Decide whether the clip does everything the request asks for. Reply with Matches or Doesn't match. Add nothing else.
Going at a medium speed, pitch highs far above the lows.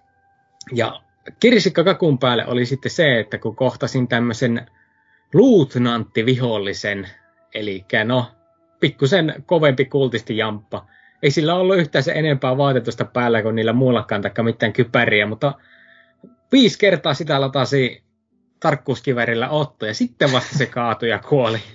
Matches